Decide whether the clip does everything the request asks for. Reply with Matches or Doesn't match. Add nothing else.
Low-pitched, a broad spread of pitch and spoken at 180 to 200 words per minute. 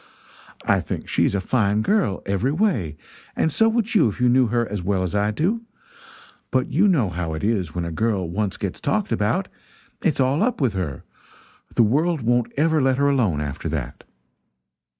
Matches